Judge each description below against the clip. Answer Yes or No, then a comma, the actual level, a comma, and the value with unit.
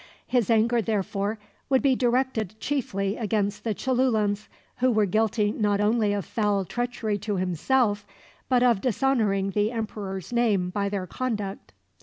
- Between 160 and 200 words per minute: No, average, 145 wpm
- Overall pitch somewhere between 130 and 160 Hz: No, high, 215 Hz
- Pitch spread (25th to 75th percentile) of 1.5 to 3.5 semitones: Yes, average, 3.2 semitones